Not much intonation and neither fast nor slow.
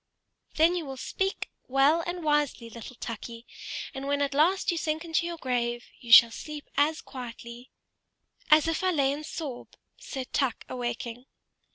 No: average, 4.6 semitones; average, 170 wpm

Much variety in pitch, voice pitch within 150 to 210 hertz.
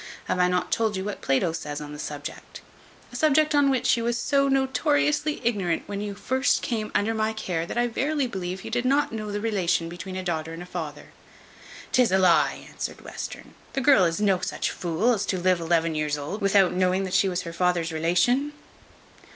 Yes: wide, 5.8 semitones; high, 190 Hz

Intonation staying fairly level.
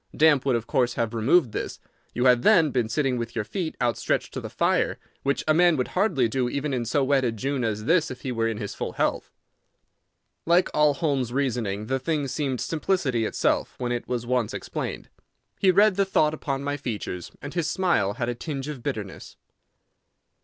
No: average, 4.3 semitones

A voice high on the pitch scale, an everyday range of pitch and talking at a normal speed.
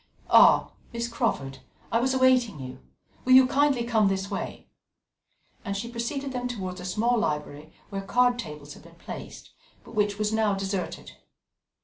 Yes: high, 215 Hz; average, 4.7 semitones; average, 160 wpm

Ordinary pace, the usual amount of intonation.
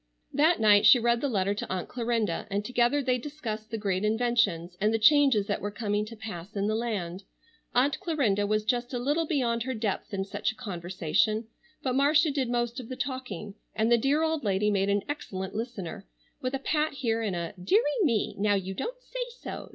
No: fast, 210 wpm; average, 4.3 semitones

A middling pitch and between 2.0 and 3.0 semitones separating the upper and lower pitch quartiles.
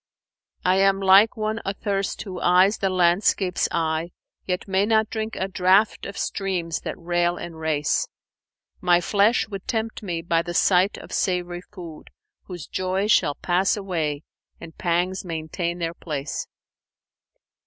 Yes: medium, 180 Hz; narrow, 2.4 semitones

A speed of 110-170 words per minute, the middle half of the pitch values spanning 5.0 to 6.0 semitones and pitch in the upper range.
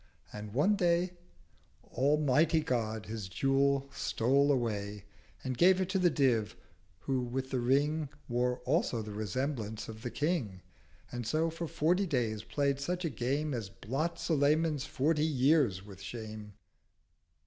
No: average, 145 wpm; wide, 5.5 semitones; low, 135 Hz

